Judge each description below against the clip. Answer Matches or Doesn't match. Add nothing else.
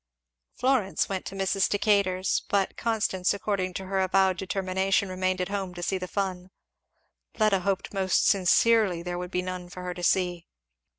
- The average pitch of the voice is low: Doesn't match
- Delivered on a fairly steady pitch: Matches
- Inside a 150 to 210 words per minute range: Matches